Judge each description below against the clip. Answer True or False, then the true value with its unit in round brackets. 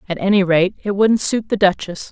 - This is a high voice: True (195 Hz)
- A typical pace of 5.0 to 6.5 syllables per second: True (5.3 syllables/s)